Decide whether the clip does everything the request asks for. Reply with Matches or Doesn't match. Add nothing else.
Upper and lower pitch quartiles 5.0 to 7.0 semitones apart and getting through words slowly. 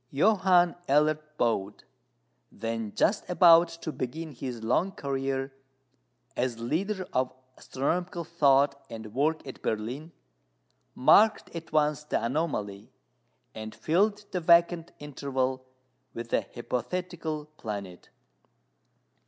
Matches